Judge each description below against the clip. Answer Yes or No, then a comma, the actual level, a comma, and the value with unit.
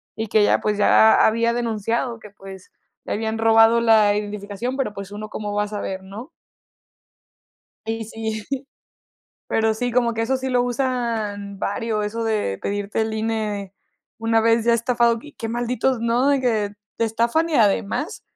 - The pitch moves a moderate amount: No, narrow, 2.2 semitones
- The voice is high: Yes, high, 225 Hz